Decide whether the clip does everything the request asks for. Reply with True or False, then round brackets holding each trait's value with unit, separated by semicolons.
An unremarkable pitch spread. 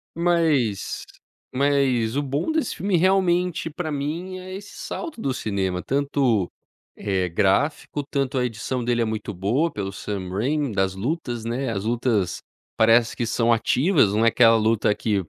False (6.1 semitones)